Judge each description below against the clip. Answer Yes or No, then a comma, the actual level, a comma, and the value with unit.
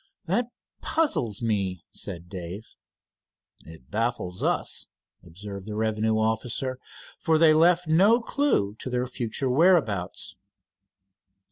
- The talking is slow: Yes, slow, 115 wpm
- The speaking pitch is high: No, low, 110 Hz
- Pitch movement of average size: No, wide, 7.9 semitones